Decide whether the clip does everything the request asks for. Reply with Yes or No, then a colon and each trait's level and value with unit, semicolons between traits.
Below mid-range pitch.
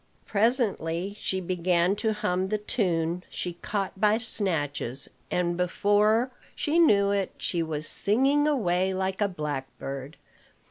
No: high, 190 Hz